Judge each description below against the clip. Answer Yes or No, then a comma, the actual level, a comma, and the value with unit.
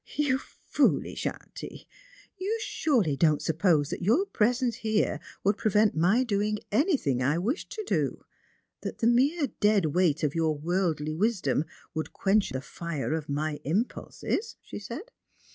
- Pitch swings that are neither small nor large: No, wide, 7.6 semitones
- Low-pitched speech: No, high, 195 Hz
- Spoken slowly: No, average, 160 wpm